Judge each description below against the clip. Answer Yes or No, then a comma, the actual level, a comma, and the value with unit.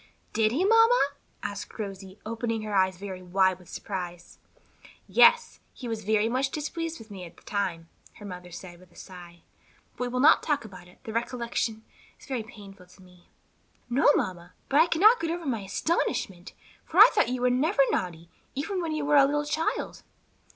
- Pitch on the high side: Yes, high, 220 Hz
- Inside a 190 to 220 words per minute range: Yes, average, 195 wpm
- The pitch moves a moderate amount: No, wide, 7.6 semitones